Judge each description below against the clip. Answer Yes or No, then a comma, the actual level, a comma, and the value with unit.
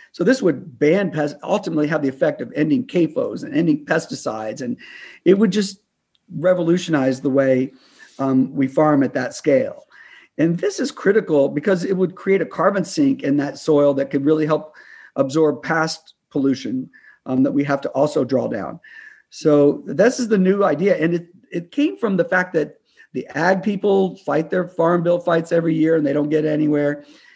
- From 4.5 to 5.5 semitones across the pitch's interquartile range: Yes, average, 4.8 semitones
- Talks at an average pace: Yes, average, 190 wpm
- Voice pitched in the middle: Yes, medium, 165 Hz